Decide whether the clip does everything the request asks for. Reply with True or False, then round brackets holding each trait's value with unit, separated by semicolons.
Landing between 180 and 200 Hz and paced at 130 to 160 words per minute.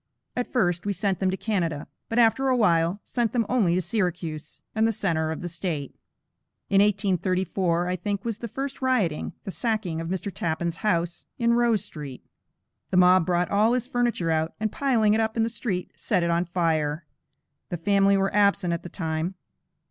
False (190 Hz; 195 wpm)